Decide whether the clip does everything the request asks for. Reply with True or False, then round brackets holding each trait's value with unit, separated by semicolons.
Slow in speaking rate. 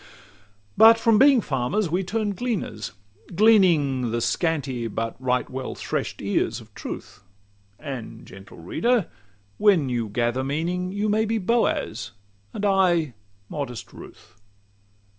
True (130 wpm)